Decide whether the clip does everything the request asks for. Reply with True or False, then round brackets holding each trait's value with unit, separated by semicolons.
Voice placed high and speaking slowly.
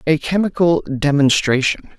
False (150 Hz; 90 wpm)